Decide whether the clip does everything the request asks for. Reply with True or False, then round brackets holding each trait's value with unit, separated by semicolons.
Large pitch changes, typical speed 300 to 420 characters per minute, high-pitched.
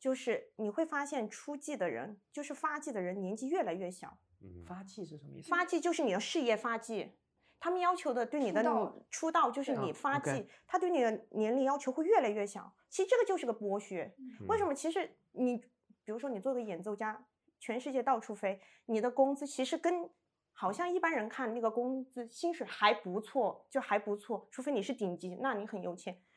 True (5.9 semitones; 305 characters per minute; 250 Hz)